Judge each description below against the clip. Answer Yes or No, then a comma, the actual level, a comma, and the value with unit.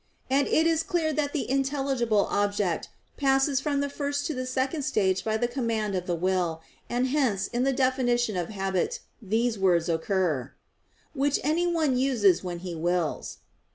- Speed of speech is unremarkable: Yes, average, 165 wpm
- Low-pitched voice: No, high, 240 Hz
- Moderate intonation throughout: No, wide, 6.6 semitones